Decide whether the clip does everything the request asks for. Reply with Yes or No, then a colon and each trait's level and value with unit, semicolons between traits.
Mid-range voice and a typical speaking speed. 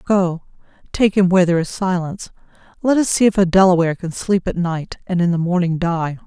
No: medium, 180 Hz; fast, 210 wpm